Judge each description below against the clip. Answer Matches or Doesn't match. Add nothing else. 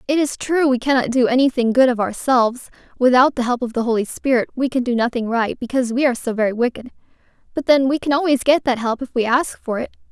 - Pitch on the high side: Matches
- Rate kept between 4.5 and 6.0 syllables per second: Doesn't match